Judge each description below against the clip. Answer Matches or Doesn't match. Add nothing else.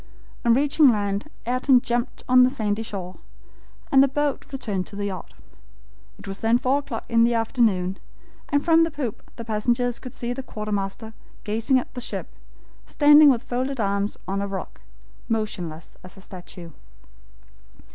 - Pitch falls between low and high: Doesn't match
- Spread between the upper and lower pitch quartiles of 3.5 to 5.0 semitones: Matches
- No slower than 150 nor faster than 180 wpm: Matches